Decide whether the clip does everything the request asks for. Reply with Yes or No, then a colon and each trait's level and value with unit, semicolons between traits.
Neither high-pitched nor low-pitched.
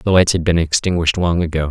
No: very low, 85 Hz